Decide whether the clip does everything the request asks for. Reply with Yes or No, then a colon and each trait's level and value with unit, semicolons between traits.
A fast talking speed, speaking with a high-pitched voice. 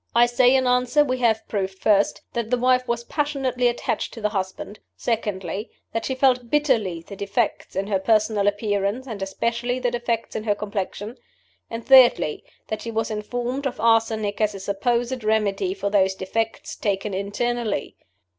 No: average, 170 wpm; high, 225 Hz